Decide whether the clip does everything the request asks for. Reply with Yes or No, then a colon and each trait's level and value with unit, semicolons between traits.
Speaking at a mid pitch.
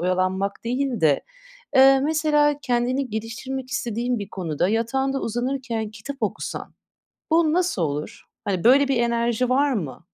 No: high, 240 Hz